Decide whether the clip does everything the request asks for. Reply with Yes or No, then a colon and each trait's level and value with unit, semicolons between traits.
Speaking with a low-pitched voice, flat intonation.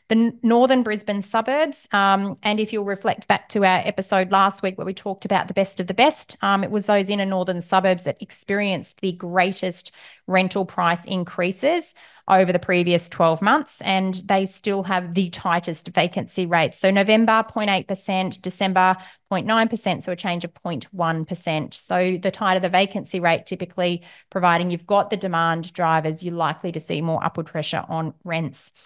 No: high, 190 Hz; narrow, 2.3 semitones